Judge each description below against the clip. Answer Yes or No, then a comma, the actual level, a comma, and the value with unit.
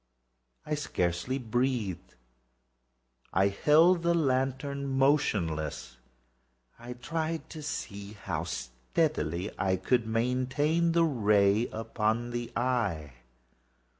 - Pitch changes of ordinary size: No, wide, 6.3 semitones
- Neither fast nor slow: No, slow, 85 wpm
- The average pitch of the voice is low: Yes, low, 120 Hz